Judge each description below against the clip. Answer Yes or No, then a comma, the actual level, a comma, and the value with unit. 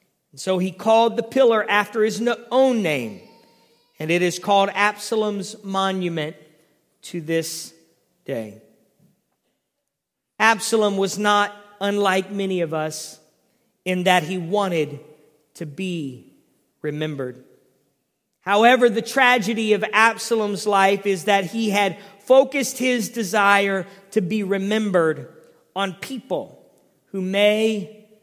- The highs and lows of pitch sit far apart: No, average, 3.4 semitones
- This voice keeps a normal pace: No, slow, 110 wpm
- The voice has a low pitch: No, high, 200 Hz